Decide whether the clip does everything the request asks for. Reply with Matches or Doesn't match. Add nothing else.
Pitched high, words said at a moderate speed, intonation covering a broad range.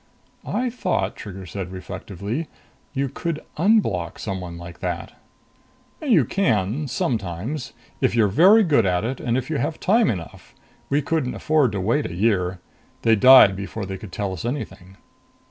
Doesn't match